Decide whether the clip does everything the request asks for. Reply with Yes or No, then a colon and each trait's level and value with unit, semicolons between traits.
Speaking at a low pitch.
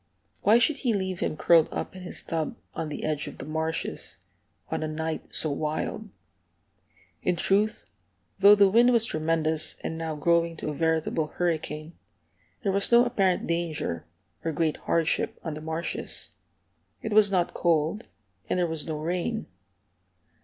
No: medium, 165 Hz